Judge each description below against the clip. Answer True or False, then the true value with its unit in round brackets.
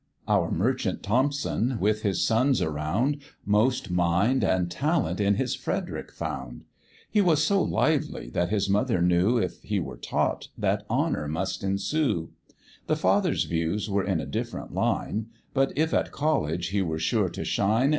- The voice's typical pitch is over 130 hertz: False (100 Hz)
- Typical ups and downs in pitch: False (6.8 semitones)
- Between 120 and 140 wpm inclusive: False (160 wpm)